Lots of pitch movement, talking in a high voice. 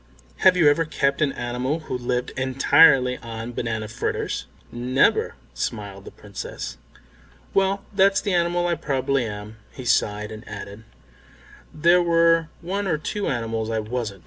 No: wide, 6.9 semitones; low, 130 Hz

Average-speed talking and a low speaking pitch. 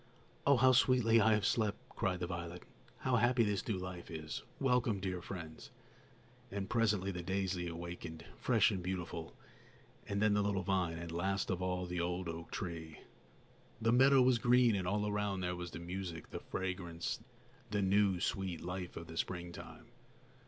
Yes: average, 175 wpm; very low, 95 Hz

